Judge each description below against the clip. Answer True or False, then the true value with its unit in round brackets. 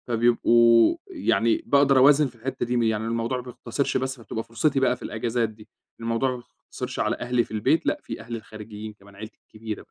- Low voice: True (115 Hz)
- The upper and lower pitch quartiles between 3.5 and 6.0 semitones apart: False (2.7 semitones)